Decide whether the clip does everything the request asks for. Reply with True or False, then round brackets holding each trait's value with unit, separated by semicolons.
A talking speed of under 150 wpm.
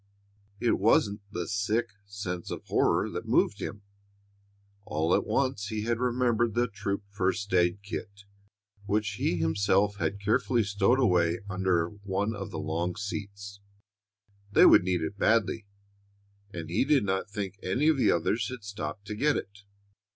False (160 wpm)